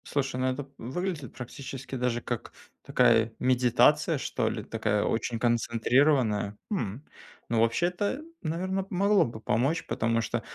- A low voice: Yes, low, 125 Hz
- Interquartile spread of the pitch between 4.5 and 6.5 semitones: Yes, average, 5.3 semitones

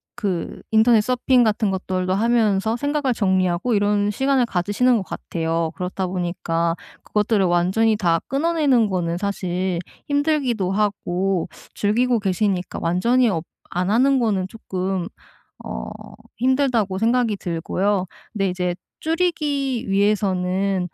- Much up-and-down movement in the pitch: No, average, 4.8 semitones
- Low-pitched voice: No, high, 205 Hz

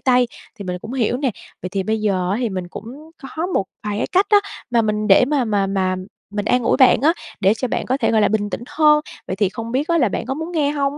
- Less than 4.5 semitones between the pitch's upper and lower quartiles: No, wide, 5.4 semitones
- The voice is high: Yes, high, 230 Hz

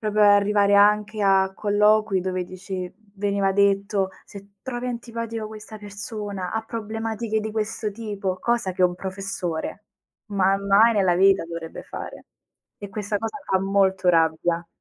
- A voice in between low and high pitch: No, high, 200 Hz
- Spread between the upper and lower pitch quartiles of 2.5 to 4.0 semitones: No, narrow, 2.0 semitones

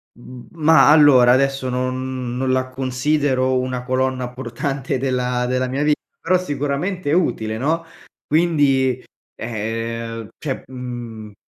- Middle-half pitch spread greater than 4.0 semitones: No, narrow, 2.4 semitones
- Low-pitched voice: Yes, low, 130 Hz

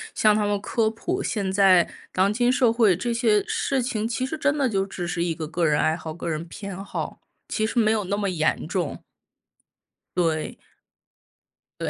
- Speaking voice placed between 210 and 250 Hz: No, high, 200 Hz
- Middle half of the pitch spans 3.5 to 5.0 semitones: Yes, average, 4.6 semitones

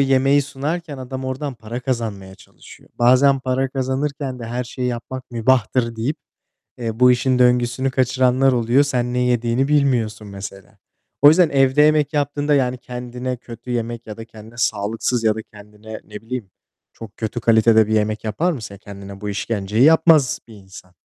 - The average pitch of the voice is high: No, low, 125 Hz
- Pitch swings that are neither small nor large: Yes, average, 3.2 semitones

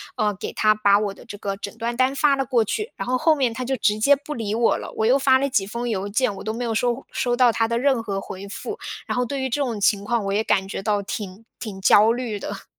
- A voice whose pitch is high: Yes, high, 230 Hz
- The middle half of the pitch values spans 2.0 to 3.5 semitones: No, average, 3.9 semitones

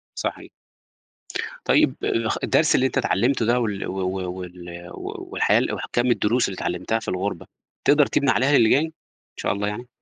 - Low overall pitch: Yes, low, 110 Hz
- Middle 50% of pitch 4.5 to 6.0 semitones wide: Yes, average, 5.2 semitones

